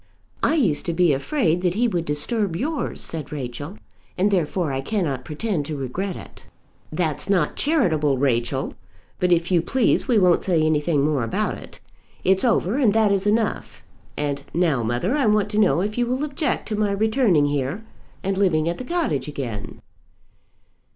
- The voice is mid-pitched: Yes, medium, 180 Hz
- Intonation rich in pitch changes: Yes, wide, 6.3 semitones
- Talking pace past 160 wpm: Yes, average, 180 wpm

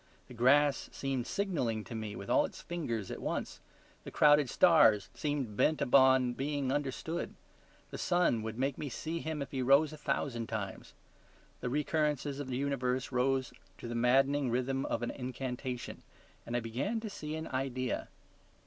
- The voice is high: No, low, 130 Hz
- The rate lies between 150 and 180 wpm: Yes, average, 170 wpm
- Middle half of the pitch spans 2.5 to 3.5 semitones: Yes, average, 3.2 semitones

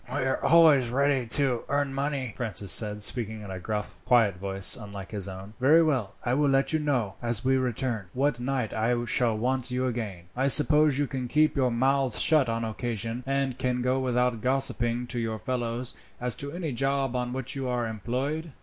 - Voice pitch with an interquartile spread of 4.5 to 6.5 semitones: No, average, 3.1 semitones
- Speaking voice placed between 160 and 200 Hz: No, low, 125 Hz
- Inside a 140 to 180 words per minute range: No, average, 200 wpm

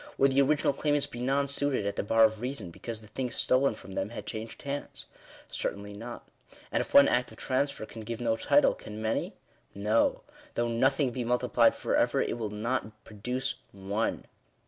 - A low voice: Yes, low, 115 Hz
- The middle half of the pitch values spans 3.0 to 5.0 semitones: Yes, average, 3.7 semitones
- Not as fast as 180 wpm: No, average, 190 wpm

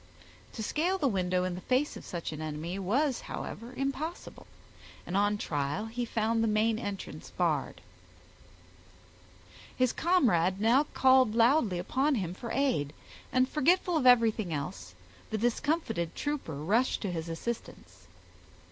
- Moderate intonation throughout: No, wide, 6.7 semitones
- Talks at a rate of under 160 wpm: Yes, average, 140 wpm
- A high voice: Yes, high, 220 Hz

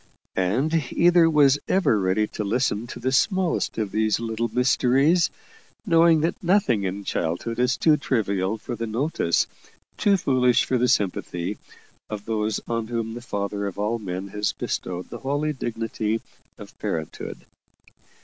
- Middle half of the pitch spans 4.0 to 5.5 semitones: Yes, average, 5.0 semitones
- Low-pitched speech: Yes, low, 115 Hz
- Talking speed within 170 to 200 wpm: No, average, 150 wpm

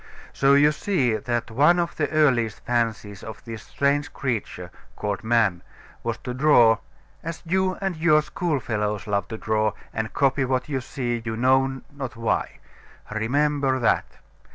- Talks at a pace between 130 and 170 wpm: Yes, average, 155 wpm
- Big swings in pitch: No, average, 4.6 semitones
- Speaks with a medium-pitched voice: No, low, 125 Hz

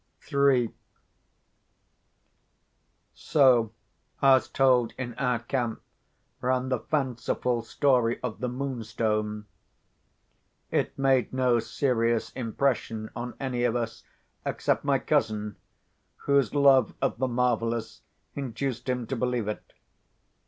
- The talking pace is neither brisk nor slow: No, slow, 105 wpm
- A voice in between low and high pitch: No, low, 125 Hz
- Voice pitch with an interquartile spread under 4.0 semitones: Yes, narrow, 2.4 semitones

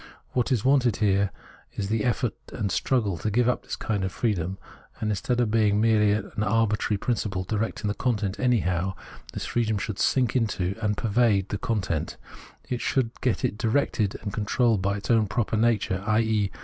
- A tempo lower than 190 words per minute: Yes, average, 175 wpm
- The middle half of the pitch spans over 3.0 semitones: No, average, 2.7 semitones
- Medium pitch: No, low, 105 Hz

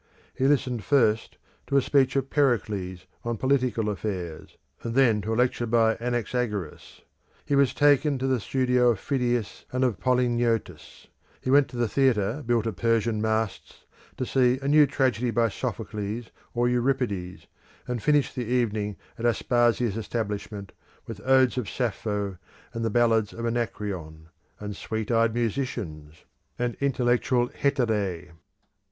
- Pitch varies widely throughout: No, average, 3.3 semitones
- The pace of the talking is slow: No, average, 145 wpm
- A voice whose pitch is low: Yes, low, 120 Hz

